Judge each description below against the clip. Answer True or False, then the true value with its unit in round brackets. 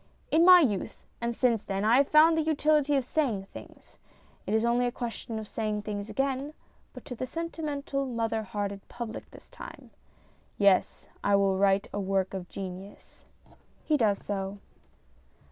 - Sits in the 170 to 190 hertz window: False (230 Hz)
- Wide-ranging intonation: True (5.7 semitones)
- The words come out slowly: False (165 wpm)